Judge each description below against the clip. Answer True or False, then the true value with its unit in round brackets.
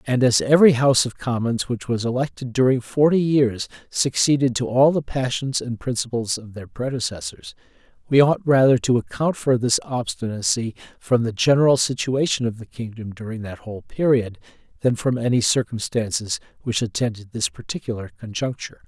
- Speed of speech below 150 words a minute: False (160 wpm)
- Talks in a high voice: False (120 Hz)